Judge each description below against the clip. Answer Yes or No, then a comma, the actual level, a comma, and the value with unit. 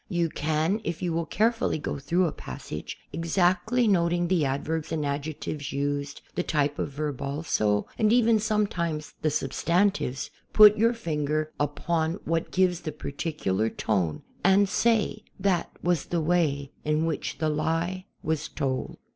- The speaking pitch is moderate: Yes, medium, 160 Hz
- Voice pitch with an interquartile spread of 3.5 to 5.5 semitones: Yes, average, 3.8 semitones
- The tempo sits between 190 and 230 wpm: No, average, 150 wpm